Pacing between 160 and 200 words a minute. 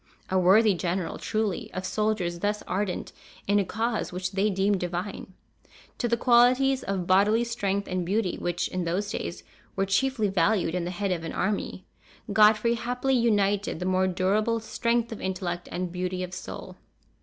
Yes: average, 170 wpm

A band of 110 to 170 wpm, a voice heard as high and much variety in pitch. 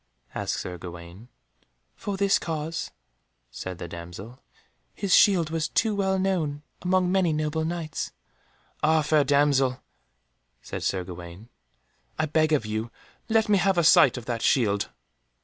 No: average, 150 wpm; medium, 150 Hz; wide, 8.1 semitones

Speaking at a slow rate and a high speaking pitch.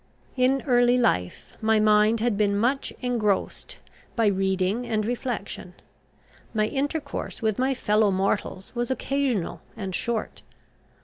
Yes: slow, 125 wpm; high, 220 Hz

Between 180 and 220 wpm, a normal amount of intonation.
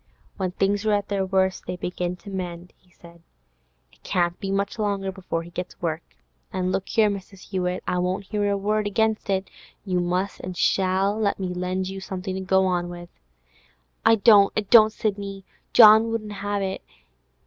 No: average, 190 wpm; narrow, 1.9 semitones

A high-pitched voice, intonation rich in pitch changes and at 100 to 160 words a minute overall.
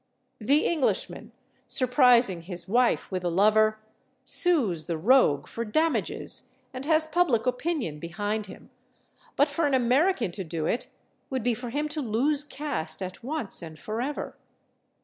Yes: high, 245 Hz; wide, 7.0 semitones; average, 150 wpm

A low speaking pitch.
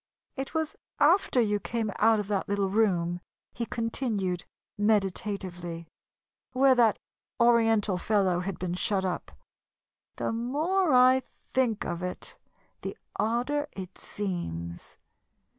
No: high, 210 Hz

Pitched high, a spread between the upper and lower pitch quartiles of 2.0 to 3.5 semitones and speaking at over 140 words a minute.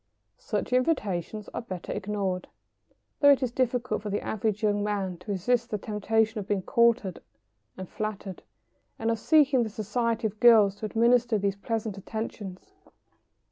Yes: high, 215 Hz; average, 2.7 semitones; average, 160 wpm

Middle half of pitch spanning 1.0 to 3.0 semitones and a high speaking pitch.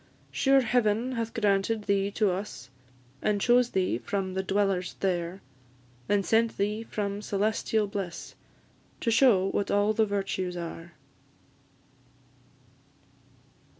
Yes: narrow, 2.5 semitones; high, 205 Hz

